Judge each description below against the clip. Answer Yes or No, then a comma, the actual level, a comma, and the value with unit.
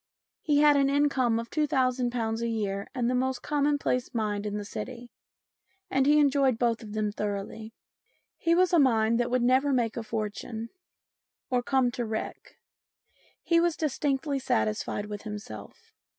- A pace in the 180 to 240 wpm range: No, average, 160 wpm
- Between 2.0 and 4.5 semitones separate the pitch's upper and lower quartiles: Yes, average, 4.1 semitones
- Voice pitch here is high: Yes, high, 245 Hz